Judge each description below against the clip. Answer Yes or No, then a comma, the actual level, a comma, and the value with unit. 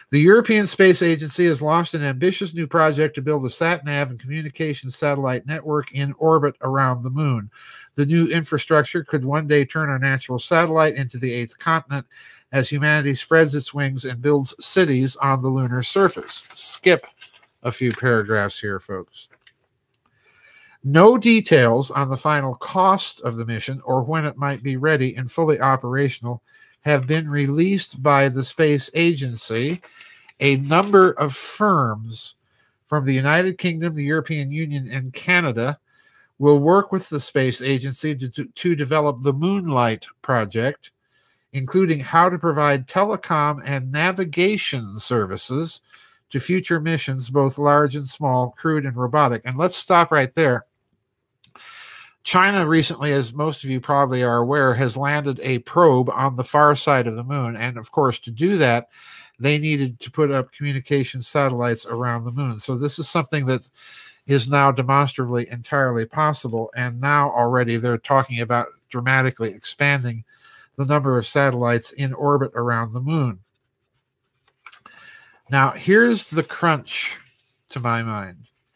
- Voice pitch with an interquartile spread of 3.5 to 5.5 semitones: Yes, average, 3.8 semitones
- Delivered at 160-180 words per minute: No, average, 150 wpm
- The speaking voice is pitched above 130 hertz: Yes, medium, 140 Hz